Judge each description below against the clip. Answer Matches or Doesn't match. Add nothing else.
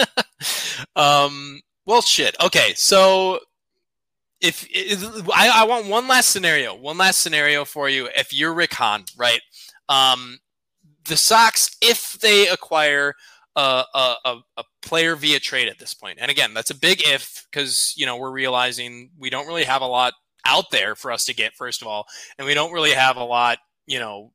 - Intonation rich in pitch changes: Matches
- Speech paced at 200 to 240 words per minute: Doesn't match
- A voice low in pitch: Doesn't match